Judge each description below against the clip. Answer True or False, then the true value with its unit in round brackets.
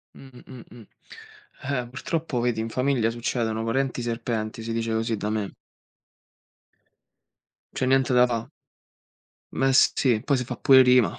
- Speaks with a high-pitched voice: False (120 Hz)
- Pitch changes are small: True (2.2 semitones)